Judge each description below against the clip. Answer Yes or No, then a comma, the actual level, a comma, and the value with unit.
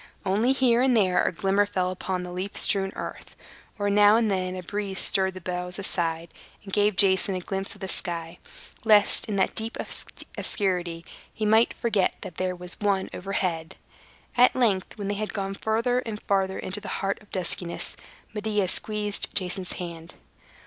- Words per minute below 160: No, average, 180 wpm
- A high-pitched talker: Yes, high, 195 Hz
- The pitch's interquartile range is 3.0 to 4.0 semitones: No, narrow, 2.4 semitones